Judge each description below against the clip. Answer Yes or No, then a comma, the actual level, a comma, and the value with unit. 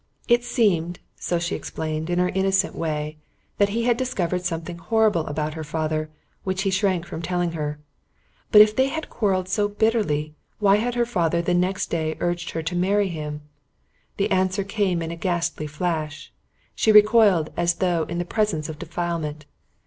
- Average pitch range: Yes, average, 4.1 semitones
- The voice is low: No, medium, 175 Hz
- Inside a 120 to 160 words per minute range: No, average, 180 wpm